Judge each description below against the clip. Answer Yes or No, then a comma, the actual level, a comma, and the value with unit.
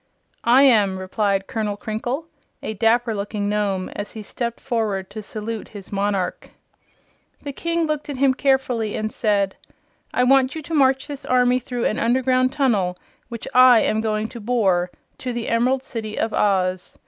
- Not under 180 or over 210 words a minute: No, average, 170 wpm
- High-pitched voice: Yes, high, 225 Hz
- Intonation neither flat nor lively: Yes, average, 3.8 semitones